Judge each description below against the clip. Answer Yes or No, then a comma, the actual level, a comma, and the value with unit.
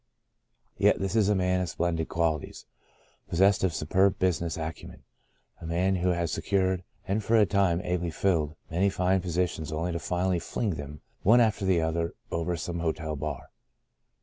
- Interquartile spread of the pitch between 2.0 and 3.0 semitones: Yes, narrow, 2.5 semitones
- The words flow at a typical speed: Yes, average, 175 wpm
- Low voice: Yes, very low, 90 Hz